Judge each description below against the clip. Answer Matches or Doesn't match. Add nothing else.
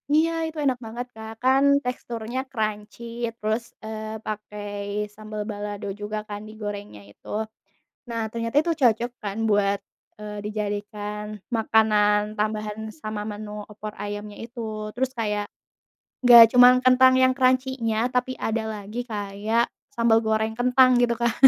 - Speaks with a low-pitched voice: Doesn't match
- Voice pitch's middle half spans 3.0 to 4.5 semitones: Doesn't match